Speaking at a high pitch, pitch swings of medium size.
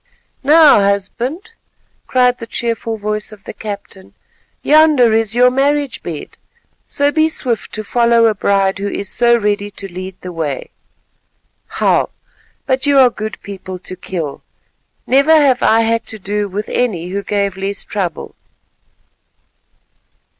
Yes: high, 215 Hz; average, 4.1 semitones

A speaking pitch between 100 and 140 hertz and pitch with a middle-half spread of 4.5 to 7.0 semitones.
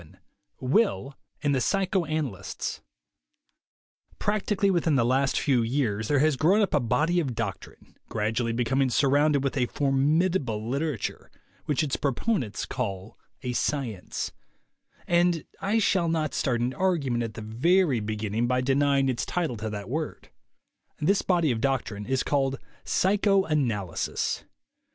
Yes: low, 135 Hz; wide, 5.6 semitones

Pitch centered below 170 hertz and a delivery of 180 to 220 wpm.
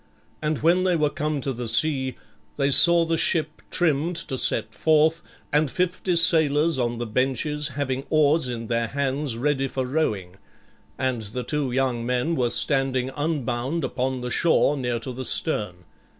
No: low, 135 Hz; average, 165 wpm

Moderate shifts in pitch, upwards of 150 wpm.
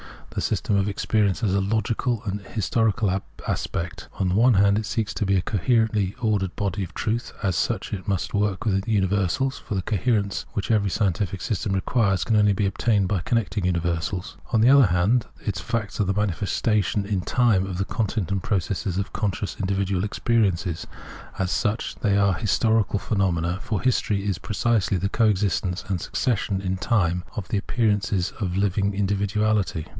No: narrow, 2.3 semitones; average, 180 wpm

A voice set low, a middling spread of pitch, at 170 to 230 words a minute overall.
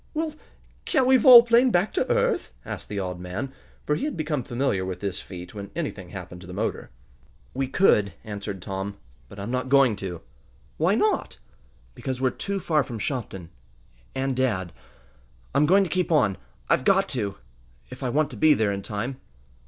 No: low, 125 Hz; wide, 7.9 semitones; average, 185 wpm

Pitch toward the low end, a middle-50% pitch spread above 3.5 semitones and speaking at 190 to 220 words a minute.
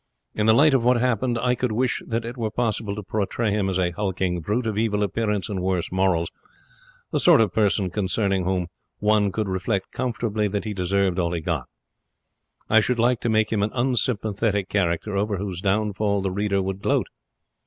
No: low, 105 Hz; average, 2.9 semitones; average, 195 wpm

